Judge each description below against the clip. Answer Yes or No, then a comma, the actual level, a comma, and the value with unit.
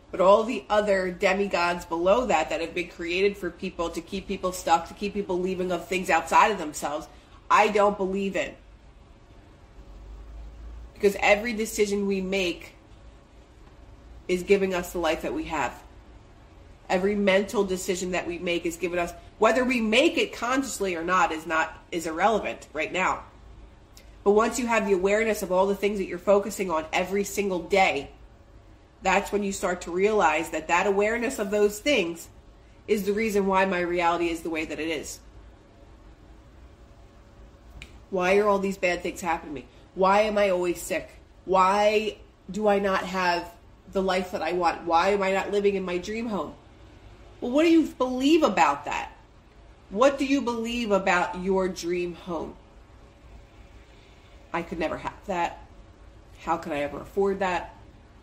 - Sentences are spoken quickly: No, average, 170 wpm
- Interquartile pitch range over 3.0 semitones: Yes, average, 3.6 semitones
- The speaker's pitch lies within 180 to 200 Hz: Yes, medium, 185 Hz